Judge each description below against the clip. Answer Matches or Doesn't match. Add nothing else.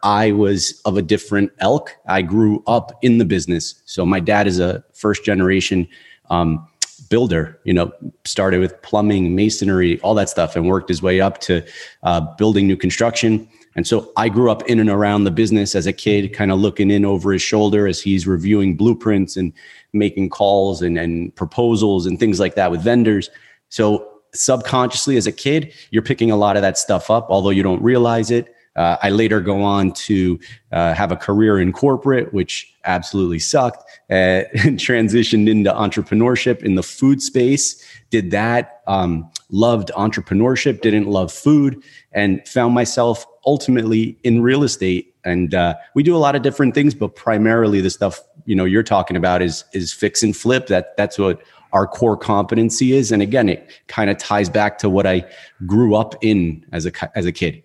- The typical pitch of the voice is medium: Doesn't match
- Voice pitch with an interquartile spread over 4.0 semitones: Doesn't match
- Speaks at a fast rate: Doesn't match